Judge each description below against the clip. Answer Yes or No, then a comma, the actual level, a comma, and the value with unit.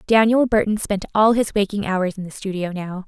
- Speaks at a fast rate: Yes, fast, 215 wpm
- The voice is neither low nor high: No, high, 200 Hz